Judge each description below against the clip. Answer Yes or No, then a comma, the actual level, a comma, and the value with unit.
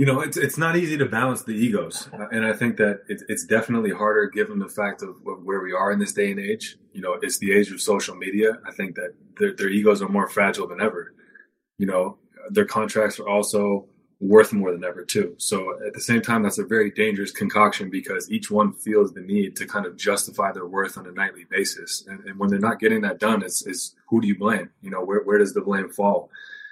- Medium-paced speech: No, fast, 240 wpm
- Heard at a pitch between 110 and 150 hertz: Yes, low, 125 Hz